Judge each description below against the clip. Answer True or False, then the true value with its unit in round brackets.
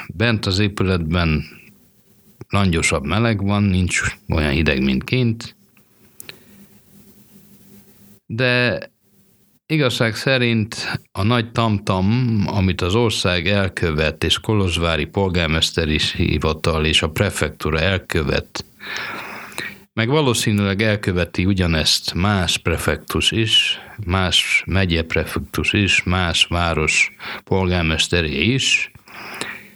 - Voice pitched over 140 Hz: False (95 Hz)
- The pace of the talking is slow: True (90 wpm)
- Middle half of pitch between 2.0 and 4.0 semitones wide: False (4.8 semitones)